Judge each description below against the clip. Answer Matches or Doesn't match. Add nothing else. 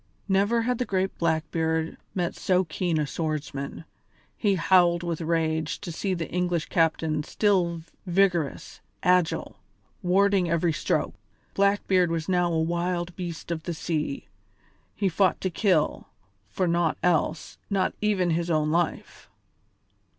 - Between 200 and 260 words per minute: Doesn't match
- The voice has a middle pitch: Matches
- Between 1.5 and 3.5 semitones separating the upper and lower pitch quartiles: Matches